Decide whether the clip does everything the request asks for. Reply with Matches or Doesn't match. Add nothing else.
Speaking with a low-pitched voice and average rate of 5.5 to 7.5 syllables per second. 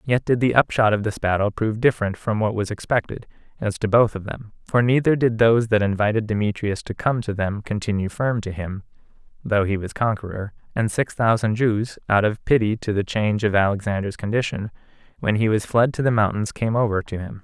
Matches